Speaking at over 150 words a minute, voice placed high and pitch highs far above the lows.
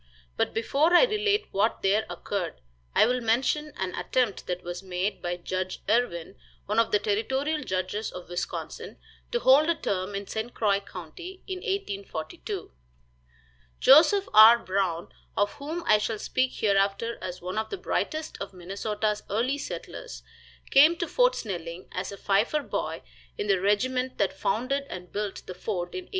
Yes: average, 165 wpm; high, 210 Hz; wide, 6.3 semitones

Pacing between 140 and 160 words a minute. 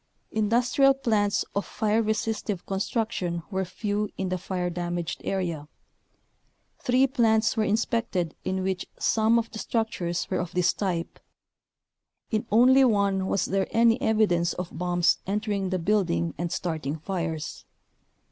Yes: average, 145 wpm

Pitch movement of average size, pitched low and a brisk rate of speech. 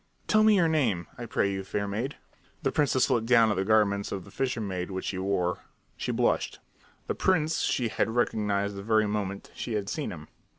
Yes: average, 4.2 semitones; low, 105 Hz; fast, 210 wpm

